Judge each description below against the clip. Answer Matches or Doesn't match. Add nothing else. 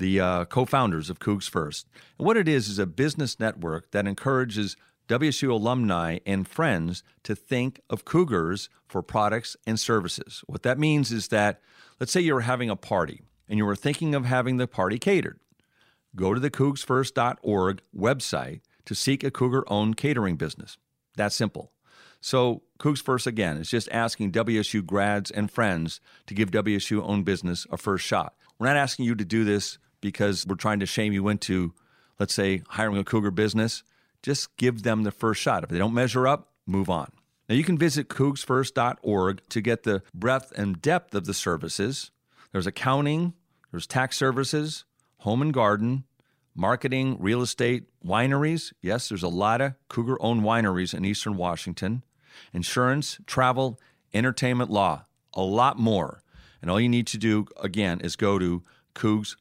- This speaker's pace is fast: Doesn't match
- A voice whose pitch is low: Matches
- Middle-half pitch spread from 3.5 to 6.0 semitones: Matches